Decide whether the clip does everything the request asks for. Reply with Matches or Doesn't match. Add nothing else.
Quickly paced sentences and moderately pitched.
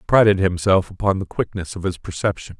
Doesn't match